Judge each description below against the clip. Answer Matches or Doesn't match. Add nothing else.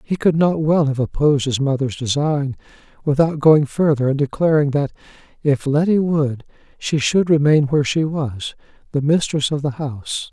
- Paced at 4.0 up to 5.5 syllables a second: Matches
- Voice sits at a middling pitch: Matches